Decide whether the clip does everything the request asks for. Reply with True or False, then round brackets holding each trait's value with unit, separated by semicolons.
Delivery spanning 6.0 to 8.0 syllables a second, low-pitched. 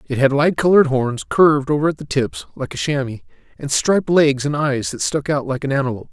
False (6.1 syllables/s; 145 Hz)